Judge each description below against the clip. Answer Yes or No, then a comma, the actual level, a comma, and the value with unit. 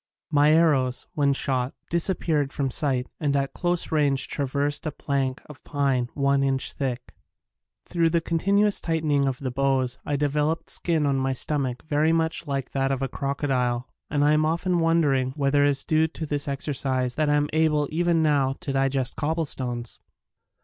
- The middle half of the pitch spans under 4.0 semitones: Yes, average, 2.7 semitones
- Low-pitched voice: No, medium, 145 Hz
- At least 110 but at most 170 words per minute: No, average, 180 wpm